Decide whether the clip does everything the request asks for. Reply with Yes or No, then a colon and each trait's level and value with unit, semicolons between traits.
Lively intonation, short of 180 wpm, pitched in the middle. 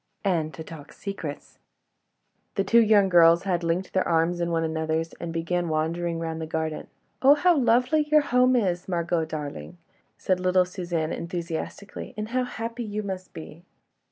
No: average, 4.0 semitones; average, 165 wpm; medium, 175 Hz